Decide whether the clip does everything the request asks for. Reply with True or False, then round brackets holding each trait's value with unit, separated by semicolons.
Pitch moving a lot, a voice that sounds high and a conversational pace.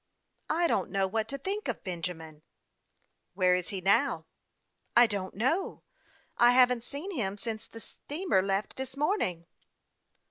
True (6.7 semitones; 220 Hz; 170 wpm)